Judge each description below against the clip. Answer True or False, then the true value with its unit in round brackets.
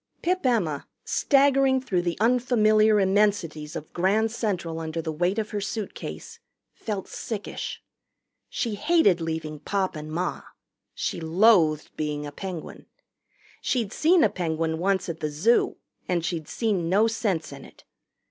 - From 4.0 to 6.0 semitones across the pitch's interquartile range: True (5.5 semitones)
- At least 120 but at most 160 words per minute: True (145 wpm)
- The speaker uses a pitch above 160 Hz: True (190 Hz)